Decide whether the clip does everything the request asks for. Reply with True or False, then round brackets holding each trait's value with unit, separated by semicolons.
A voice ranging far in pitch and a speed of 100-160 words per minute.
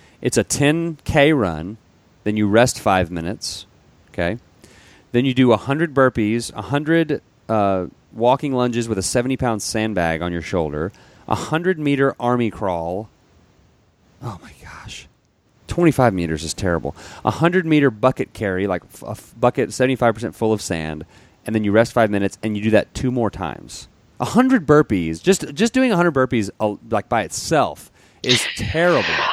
True (5.7 semitones; 155 wpm)